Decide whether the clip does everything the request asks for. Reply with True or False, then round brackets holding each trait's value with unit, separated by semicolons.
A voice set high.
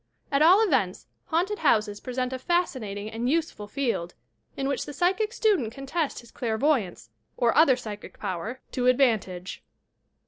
True (255 Hz)